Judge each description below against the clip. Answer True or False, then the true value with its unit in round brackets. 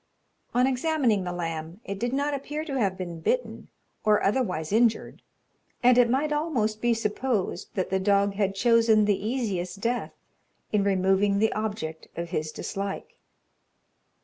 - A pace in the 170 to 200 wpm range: False (150 wpm)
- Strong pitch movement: False (4.4 semitones)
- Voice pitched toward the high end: True (210 Hz)